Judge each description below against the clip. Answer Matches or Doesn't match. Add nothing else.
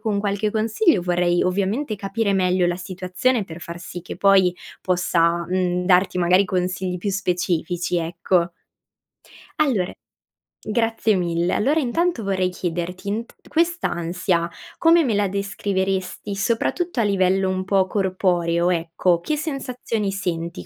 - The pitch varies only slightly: Doesn't match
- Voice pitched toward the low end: Doesn't match